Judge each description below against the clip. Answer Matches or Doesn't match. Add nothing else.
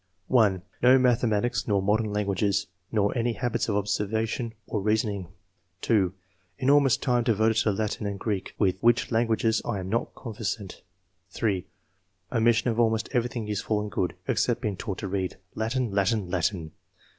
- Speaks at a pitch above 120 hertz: Doesn't match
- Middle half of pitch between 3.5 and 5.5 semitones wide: Doesn't match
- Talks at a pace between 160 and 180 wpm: Matches